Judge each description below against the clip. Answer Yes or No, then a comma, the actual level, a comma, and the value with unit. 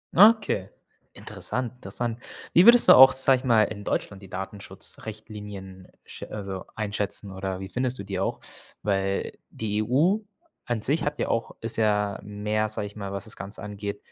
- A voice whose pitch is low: Yes, low, 105 Hz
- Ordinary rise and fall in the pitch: Yes, average, 3.4 semitones